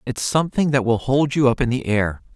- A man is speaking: Yes, male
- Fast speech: Yes, fast, 255 wpm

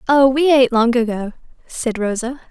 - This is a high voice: Yes, high, 245 Hz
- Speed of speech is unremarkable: Yes, average, 165 wpm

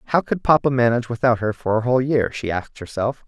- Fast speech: Yes, fast, 240 wpm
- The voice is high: No, low, 120 Hz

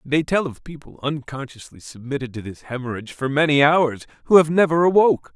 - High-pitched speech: No, medium, 145 Hz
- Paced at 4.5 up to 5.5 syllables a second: No, 5.8 syllables/s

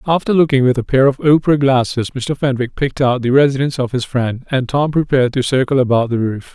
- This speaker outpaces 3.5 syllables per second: Yes, 6.2 syllables/s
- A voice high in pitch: No, low, 130 Hz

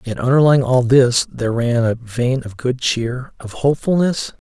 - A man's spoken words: Yes, male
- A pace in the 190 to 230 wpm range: No, average, 175 wpm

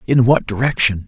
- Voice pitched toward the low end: Yes, low, 120 Hz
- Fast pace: No, average, 165 wpm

